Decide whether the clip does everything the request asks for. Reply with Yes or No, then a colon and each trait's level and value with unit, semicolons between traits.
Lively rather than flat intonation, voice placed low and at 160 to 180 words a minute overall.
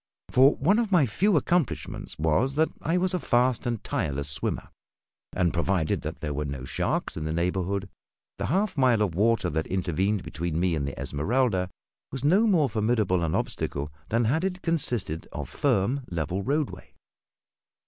Yes: wide, 9.0 semitones; low, 105 Hz; average, 170 wpm